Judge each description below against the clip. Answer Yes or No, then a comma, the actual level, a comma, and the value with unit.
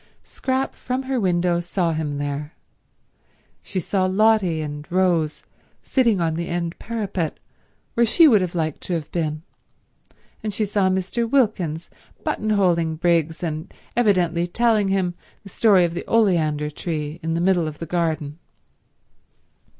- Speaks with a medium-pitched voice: Yes, medium, 175 Hz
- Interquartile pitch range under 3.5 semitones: No, average, 4.1 semitones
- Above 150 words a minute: No, average, 145 wpm